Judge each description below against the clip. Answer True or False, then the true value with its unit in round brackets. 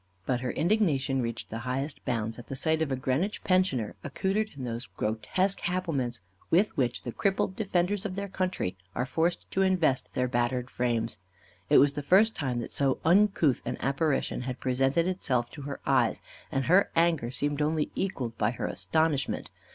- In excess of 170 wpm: True (180 wpm)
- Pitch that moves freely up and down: True (6.3 semitones)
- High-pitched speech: False (140 Hz)